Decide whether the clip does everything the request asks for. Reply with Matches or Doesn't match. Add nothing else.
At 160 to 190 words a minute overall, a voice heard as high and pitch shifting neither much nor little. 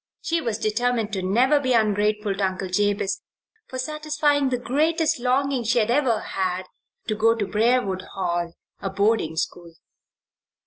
Doesn't match